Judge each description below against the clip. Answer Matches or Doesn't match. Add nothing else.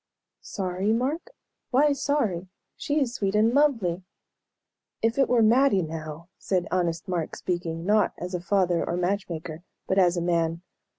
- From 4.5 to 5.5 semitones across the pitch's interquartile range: Matches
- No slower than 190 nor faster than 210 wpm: Doesn't match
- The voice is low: Doesn't match